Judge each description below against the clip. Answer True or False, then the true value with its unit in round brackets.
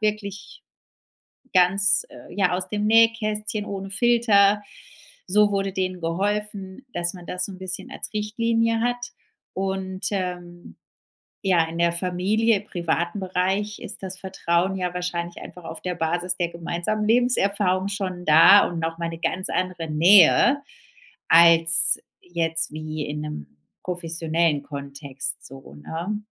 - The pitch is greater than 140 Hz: True (185 Hz)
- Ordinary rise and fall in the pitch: True (3.4 semitones)